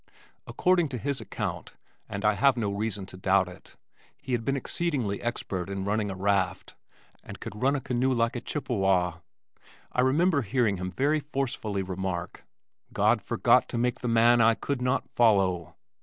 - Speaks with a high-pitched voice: No, low, 115 Hz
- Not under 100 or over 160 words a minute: No, average, 170 wpm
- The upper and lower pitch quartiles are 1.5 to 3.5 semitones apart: No, average, 5.2 semitones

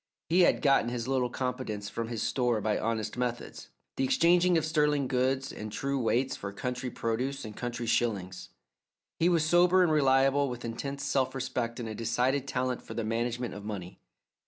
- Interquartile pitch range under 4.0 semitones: Yes, average, 3.2 semitones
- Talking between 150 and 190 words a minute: Yes, average, 180 wpm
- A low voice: Yes, low, 125 Hz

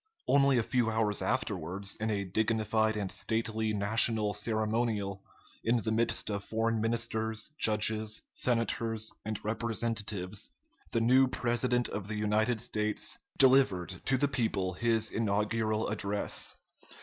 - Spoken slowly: Yes, slow, 125 wpm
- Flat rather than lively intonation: Yes, narrow, 1.6 semitones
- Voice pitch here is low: Yes, low, 110 Hz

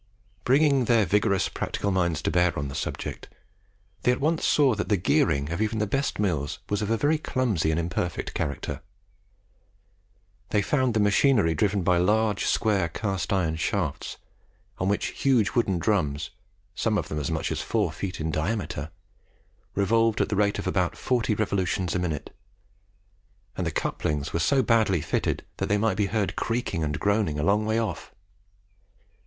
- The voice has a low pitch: Yes, low, 100 Hz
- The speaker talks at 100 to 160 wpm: No, average, 175 wpm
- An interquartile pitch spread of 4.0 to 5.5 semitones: Yes, average, 4.8 semitones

